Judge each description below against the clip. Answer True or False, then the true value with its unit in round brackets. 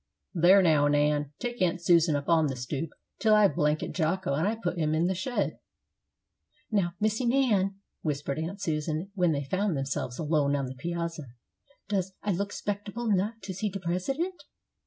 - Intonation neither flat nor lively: True (4.9 semitones)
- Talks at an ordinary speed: True (175 wpm)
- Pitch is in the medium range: True (175 Hz)